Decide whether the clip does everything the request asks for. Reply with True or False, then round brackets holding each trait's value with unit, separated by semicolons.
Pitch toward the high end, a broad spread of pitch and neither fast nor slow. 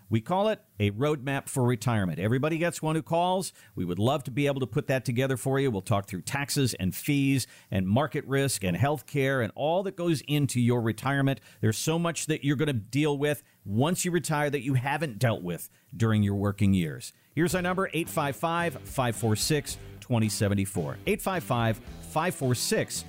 False (135 Hz; 5.9 semitones; 185 wpm)